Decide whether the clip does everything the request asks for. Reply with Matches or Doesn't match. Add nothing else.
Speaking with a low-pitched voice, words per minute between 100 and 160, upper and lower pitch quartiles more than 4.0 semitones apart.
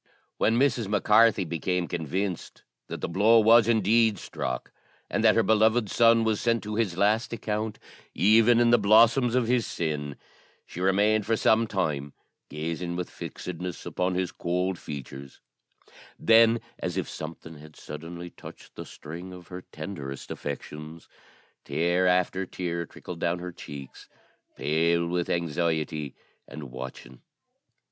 Matches